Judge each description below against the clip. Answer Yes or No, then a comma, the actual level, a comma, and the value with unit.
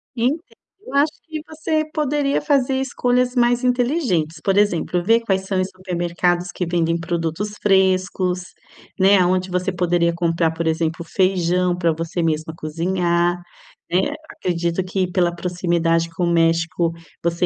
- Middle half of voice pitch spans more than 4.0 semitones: No, average, 3.2 semitones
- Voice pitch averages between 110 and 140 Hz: No, medium, 180 Hz